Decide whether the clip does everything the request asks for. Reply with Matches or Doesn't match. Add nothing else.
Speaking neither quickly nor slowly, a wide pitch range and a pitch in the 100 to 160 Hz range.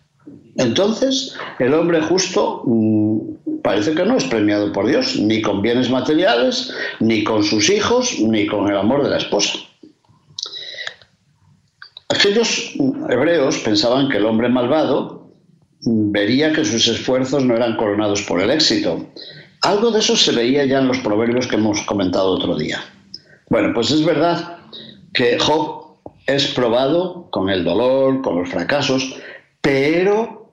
Matches